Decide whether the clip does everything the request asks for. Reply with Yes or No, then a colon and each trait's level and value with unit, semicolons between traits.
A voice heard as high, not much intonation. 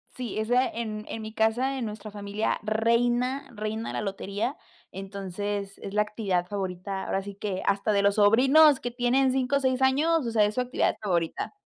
No: high, 215 Hz; average, 3.8 semitones